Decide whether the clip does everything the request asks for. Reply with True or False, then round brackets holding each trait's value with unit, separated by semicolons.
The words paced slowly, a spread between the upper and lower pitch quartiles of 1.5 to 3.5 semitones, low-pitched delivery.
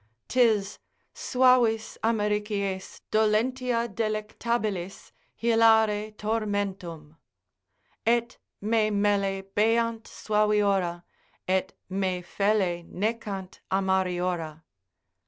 False (65 wpm; 2.8 semitones; 210 Hz)